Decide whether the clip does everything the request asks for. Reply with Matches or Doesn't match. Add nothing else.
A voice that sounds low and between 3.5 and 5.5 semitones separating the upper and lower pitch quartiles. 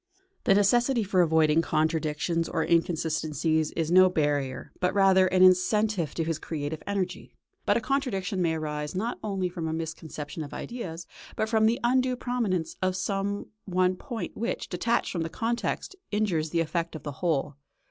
Doesn't match